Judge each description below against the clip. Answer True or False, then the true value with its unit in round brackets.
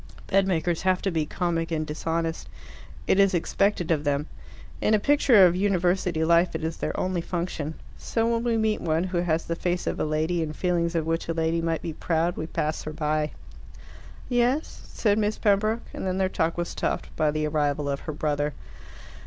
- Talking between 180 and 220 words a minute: True (200 wpm)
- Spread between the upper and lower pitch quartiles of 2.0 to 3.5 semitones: True (3.2 semitones)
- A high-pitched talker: False (170 Hz)